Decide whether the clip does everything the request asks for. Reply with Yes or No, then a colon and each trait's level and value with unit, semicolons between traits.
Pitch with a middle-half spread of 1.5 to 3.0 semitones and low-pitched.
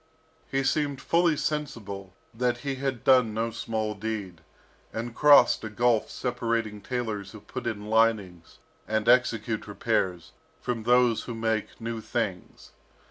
Yes: narrow, 2.5 semitones; low, 115 Hz